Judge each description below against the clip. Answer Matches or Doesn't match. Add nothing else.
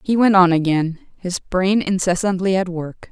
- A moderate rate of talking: Matches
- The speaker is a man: Doesn't match